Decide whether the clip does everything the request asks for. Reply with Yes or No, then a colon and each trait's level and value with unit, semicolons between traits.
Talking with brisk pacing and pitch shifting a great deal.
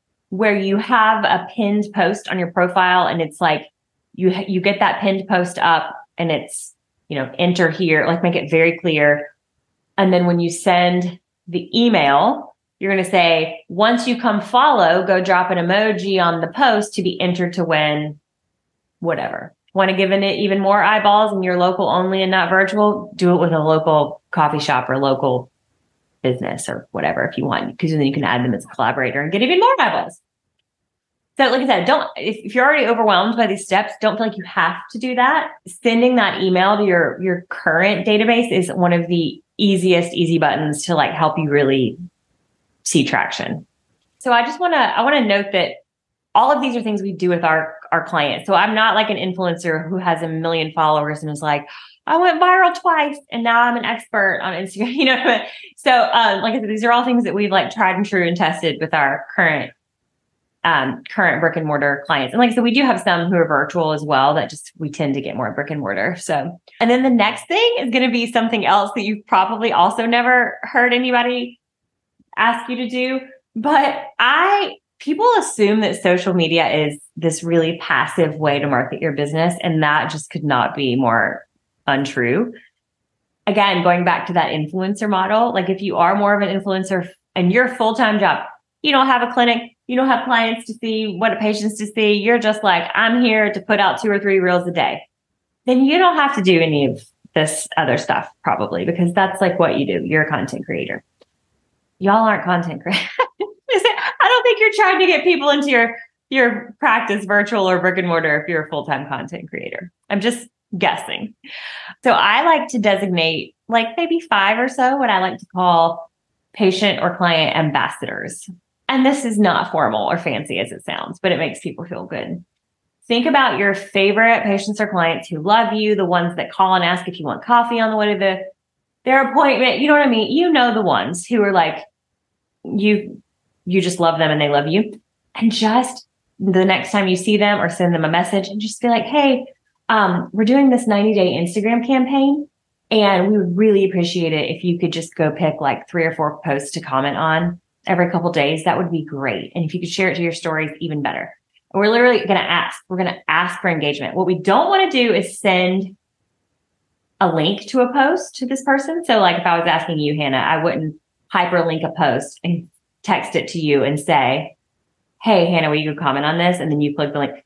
Yes: fast, 215 wpm; wide, 5.8 semitones